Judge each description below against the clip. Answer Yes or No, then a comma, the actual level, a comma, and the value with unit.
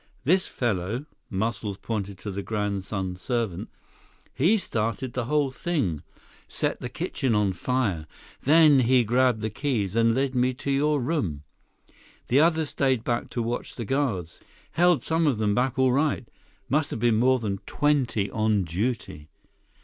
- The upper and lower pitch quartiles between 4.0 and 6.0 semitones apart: Yes, average, 4.9 semitones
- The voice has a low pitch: Yes, low, 120 Hz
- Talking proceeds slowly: No, average, 155 wpm